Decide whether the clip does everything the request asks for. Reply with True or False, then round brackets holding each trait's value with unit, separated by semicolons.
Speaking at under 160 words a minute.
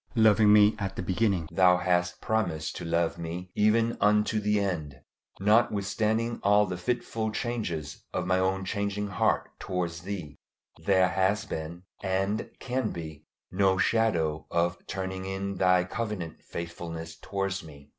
True (145 wpm)